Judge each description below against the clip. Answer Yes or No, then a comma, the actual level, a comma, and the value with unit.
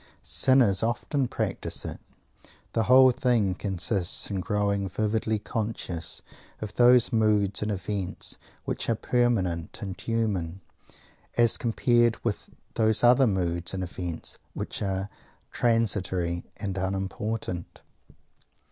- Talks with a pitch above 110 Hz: No, low, 105 Hz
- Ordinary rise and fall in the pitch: Yes, average, 3.6 semitones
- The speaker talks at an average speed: No, slow, 110 wpm